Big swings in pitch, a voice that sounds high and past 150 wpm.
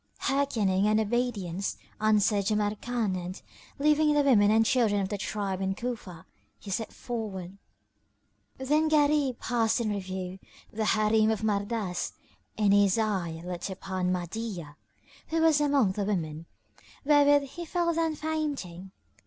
No: wide, 5.7 semitones; high, 215 Hz; slow, 135 wpm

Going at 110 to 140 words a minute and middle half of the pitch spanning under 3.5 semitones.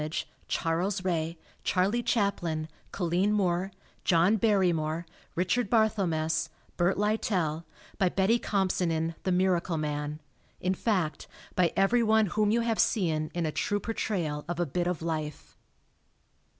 No: slow, 135 wpm; average, 3.9 semitones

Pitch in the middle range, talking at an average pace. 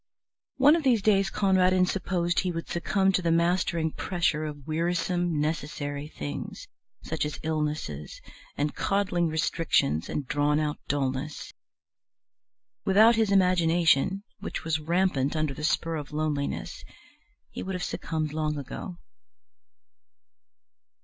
No: medium, 165 Hz; slow, 125 wpm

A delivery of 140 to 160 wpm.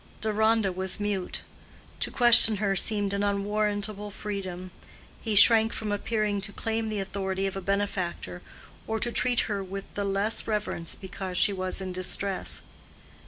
Yes: average, 155 wpm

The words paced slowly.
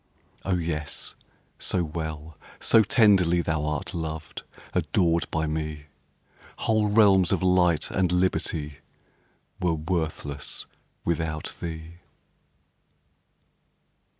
Yes: slow, 90 wpm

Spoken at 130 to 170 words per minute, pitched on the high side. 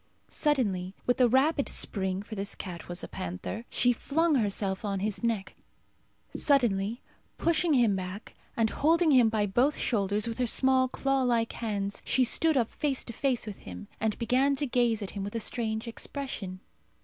No: average, 180 wpm; high, 230 Hz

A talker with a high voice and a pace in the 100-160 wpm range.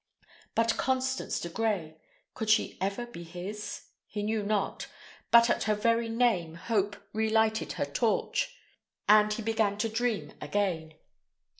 Yes: high, 215 Hz; average, 140 wpm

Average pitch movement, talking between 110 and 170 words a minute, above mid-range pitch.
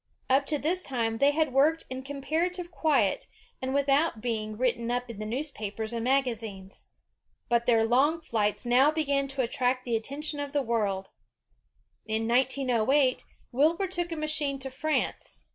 Yes: average, 4.1 semitones; average, 165 wpm; very high, 265 Hz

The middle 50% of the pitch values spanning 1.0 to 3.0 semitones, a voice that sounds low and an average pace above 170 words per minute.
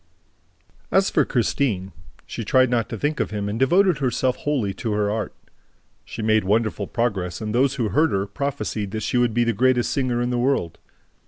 No: average, 3.6 semitones; low, 120 Hz; average, 195 wpm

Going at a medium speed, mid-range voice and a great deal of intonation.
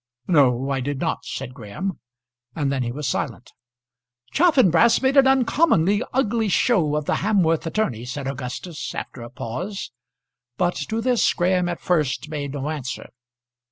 Yes: average, 155 wpm; medium, 160 Hz; wide, 7.2 semitones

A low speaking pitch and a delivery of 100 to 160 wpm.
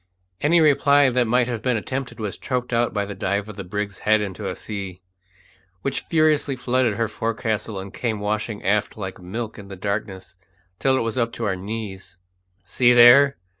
No: low, 110 Hz; average, 190 wpm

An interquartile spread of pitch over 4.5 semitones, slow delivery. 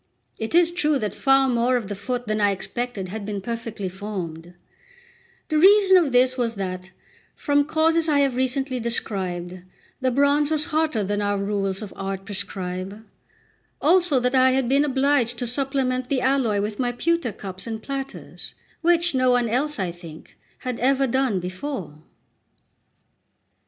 No: wide, 5.4 semitones; average, 160 wpm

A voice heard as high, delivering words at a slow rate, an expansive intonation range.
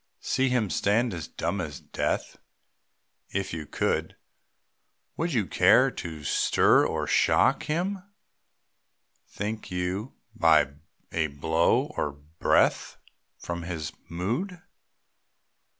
No: very low, 90 Hz; slow, 105 wpm; wide, 7.3 semitones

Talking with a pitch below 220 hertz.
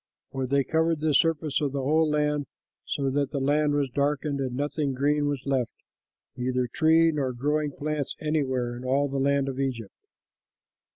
Yes: medium, 140 Hz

